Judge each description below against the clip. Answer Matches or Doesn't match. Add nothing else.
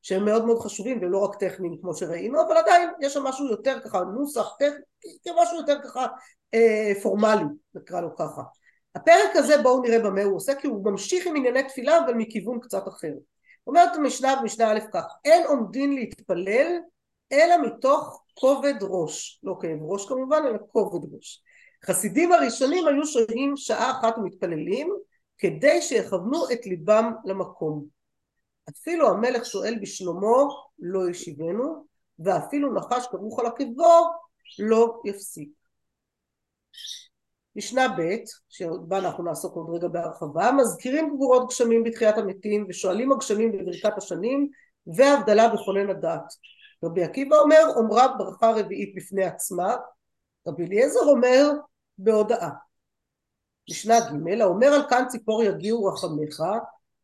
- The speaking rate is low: Doesn't match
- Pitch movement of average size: Doesn't match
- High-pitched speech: Matches